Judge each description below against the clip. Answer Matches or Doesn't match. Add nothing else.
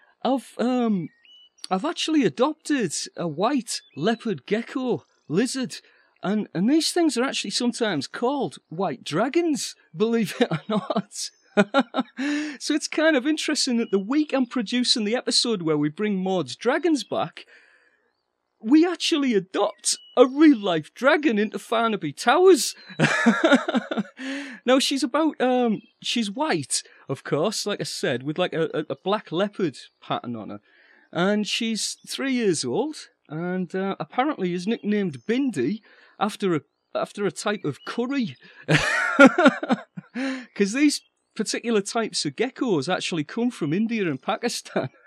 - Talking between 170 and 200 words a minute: Doesn't match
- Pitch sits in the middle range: Doesn't match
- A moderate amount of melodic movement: Doesn't match